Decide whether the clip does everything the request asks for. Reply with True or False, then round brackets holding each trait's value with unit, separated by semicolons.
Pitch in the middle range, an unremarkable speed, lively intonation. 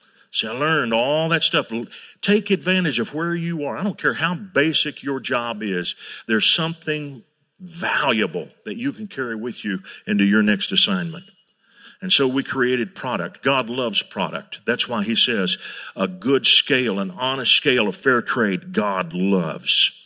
True (150 Hz; 170 wpm; 7.3 semitones)